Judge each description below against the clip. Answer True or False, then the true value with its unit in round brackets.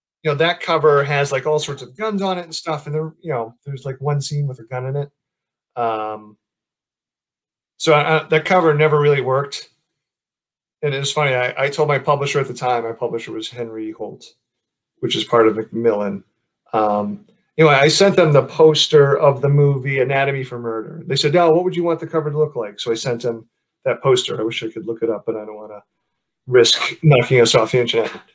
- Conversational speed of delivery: False (225 wpm)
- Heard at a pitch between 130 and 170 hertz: True (140 Hz)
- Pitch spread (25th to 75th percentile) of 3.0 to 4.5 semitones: False (4.9 semitones)